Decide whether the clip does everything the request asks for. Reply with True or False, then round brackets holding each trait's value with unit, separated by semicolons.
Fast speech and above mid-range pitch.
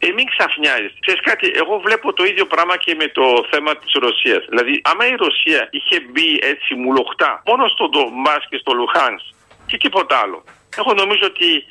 True (185 wpm; 200 Hz)